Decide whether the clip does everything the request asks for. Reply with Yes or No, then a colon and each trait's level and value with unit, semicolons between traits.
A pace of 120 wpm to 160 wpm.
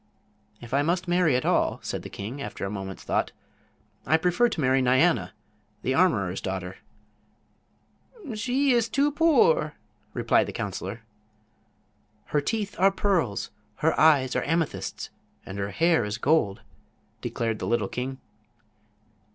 Yes: average, 140 wpm